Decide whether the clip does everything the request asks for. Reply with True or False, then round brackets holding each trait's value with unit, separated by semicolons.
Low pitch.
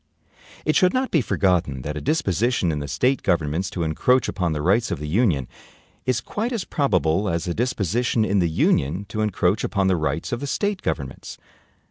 True (95 Hz)